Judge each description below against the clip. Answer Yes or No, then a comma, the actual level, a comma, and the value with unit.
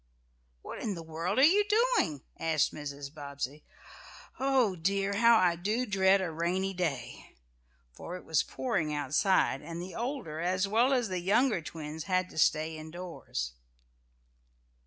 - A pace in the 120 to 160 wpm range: Yes, average, 155 wpm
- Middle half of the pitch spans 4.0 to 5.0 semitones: Yes, average, 4.4 semitones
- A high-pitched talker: No, medium, 180 Hz